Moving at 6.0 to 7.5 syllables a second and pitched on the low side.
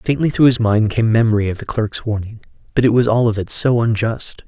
No: 5.6 syllables/s; low, 115 Hz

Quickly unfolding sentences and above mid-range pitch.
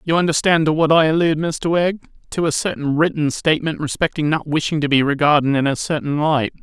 No: fast, 210 wpm; medium, 155 Hz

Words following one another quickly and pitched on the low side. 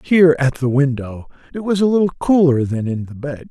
No: fast, 220 wpm; medium, 145 Hz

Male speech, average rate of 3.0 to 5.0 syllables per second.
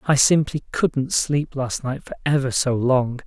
Yes: male; 4.1 syllables/s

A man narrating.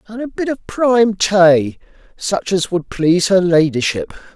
Yes: male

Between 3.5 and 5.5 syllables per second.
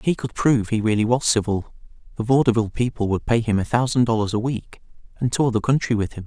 No: 6.5 syllables/s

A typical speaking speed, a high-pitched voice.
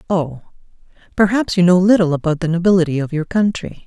No: average, 170 wpm; medium, 175 Hz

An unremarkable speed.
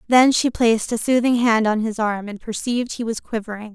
No: fast, 225 wpm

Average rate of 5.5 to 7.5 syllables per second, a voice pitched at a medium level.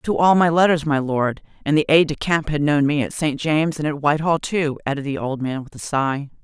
Yes: 5.6 syllables/s; medium, 150 Hz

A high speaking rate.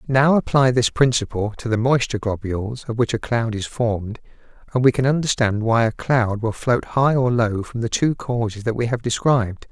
Yes: fast, 210 wpm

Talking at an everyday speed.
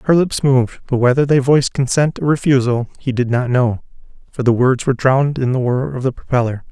No: fast, 225 wpm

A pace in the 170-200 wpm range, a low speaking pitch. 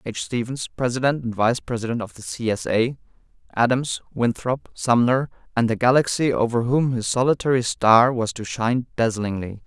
No: average, 160 wpm; low, 120 Hz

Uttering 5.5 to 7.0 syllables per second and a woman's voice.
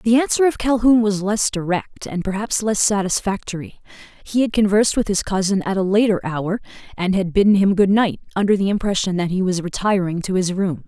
Yes: 5.6 syllables/s; female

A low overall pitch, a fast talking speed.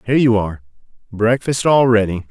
No: low, 110 Hz; average, 155 wpm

